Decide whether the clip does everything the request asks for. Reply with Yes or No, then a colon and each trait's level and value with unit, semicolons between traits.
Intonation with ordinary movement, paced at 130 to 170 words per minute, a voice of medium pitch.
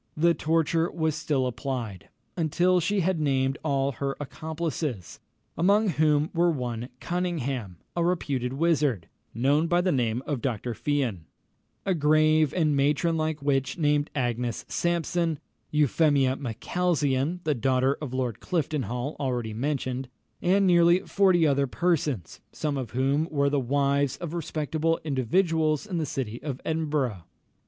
Yes: average, 3.9 semitones; average, 140 wpm; medium, 145 Hz